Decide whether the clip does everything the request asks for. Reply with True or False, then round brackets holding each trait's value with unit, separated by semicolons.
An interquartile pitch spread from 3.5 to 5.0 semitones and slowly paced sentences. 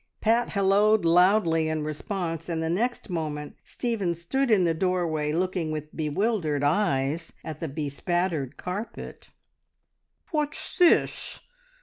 True (4.7 semitones; 120 wpm)